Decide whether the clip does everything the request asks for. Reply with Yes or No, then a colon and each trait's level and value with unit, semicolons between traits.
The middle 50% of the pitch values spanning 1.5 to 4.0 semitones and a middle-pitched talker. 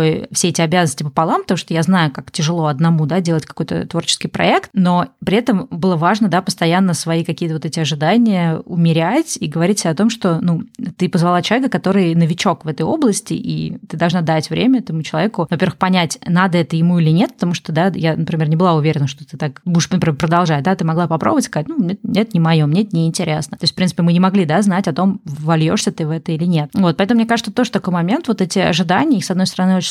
Yes: average, 2.9 semitones; medium, 175 Hz